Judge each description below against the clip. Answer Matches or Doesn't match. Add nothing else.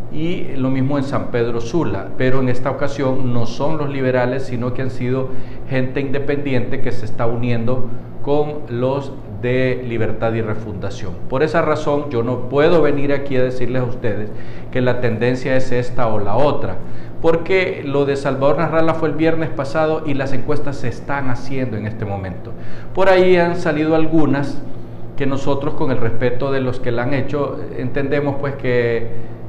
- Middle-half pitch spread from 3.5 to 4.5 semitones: Doesn't match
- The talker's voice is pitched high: Doesn't match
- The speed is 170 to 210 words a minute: Matches